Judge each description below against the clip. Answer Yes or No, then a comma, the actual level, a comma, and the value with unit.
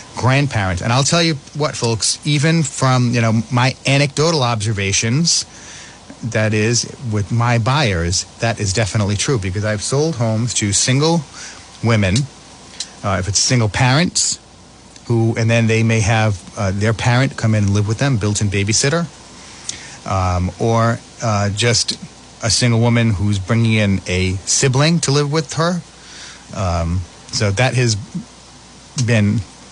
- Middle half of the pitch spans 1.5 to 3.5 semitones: No, average, 4.0 semitones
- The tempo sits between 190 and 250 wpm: No, average, 145 wpm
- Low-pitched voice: Yes, low, 115 Hz